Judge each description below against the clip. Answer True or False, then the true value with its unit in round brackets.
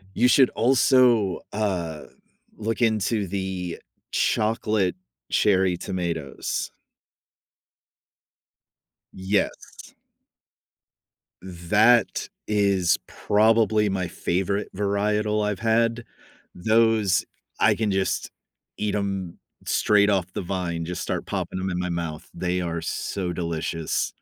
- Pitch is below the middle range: True (100 Hz)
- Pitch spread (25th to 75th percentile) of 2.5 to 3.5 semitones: True (3.2 semitones)